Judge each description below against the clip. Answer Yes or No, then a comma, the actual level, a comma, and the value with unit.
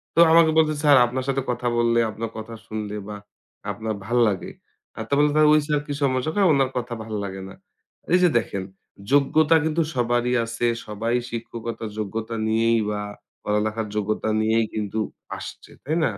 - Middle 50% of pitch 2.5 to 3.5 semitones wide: No, average, 4.3 semitones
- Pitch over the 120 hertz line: No, low, 115 Hz